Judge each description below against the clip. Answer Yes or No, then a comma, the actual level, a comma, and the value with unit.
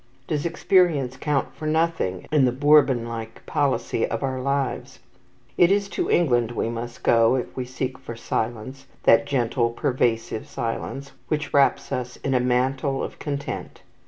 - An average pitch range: Yes, average, 3.3 semitones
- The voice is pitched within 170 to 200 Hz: No, low, 130 Hz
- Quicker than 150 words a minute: Yes, average, 160 wpm